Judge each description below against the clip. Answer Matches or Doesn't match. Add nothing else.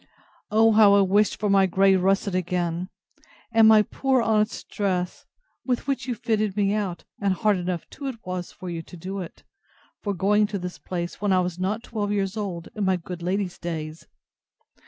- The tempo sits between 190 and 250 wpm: Matches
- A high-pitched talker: Matches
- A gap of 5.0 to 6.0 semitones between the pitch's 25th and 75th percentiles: Doesn't match